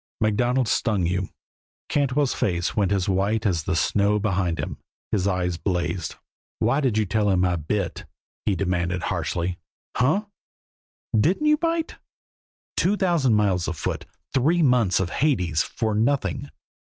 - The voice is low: Yes, low, 105 Hz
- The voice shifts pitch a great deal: Yes, wide, 6.0 semitones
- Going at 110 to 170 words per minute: Yes, average, 140 wpm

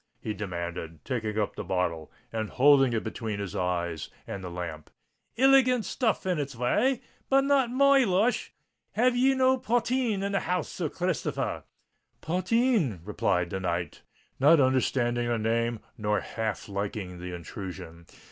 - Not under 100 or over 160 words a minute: Yes, average, 150 wpm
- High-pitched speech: No, low, 120 Hz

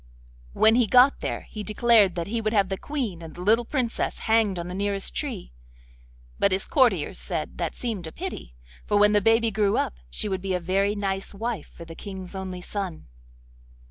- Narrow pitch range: No, average, 3.5 semitones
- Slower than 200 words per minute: No, fast, 205 wpm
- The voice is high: Yes, high, 200 Hz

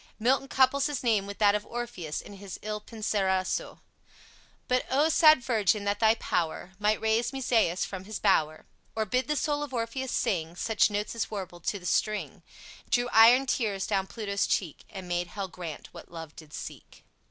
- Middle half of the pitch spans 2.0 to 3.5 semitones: No, average, 4.2 semitones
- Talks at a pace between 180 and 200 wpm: Yes, average, 185 wpm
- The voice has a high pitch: Yes, high, 210 Hz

